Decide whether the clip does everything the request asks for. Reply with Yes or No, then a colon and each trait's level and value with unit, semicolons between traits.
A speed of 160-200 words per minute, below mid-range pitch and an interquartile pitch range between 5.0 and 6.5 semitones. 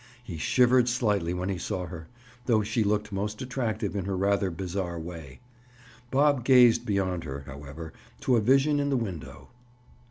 Yes: average, 165 wpm; low, 100 Hz; wide, 5.6 semitones